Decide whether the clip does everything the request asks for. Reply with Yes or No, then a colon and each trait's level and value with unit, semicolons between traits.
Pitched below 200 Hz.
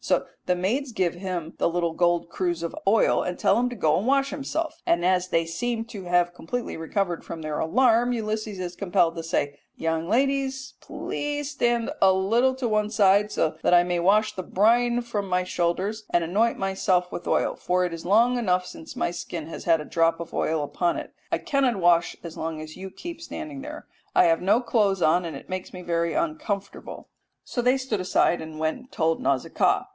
Yes: medium, 185 Hz